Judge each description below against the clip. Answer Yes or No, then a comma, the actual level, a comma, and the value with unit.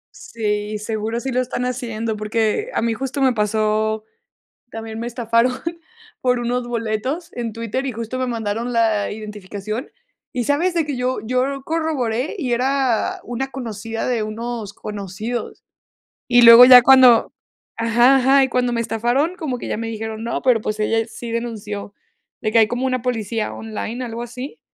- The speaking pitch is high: Yes, high, 235 Hz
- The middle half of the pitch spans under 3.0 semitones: Yes, narrow, 2.5 semitones